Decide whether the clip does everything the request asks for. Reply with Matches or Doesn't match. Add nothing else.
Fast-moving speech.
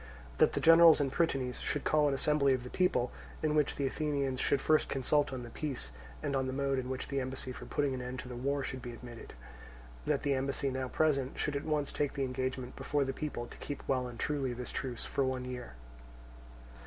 Matches